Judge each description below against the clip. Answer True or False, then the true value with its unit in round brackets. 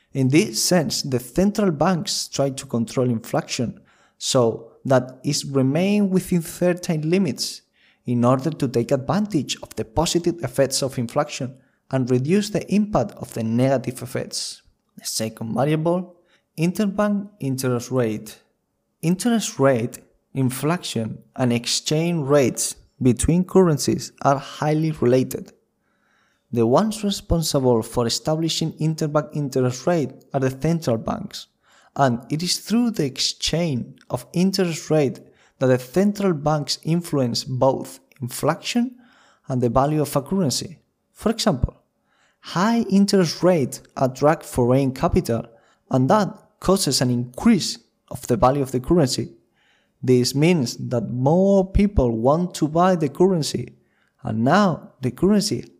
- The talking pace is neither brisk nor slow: False (130 wpm)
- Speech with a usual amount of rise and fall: False (5.7 semitones)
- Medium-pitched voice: True (150 Hz)